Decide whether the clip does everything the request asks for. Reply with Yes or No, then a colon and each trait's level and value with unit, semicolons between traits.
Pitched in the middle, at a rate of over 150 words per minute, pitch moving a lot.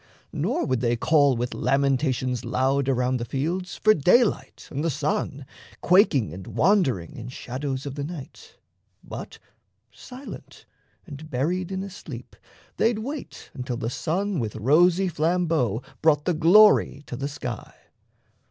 No: medium, 145 Hz; average, 145 wpm; wide, 5.9 semitones